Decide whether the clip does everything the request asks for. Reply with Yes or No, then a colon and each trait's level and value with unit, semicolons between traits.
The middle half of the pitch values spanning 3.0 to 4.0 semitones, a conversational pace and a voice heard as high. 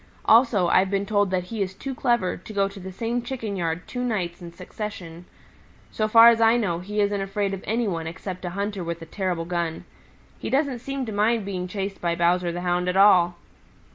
No: average, 3.7 semitones; fast, 220 wpm; high, 195 Hz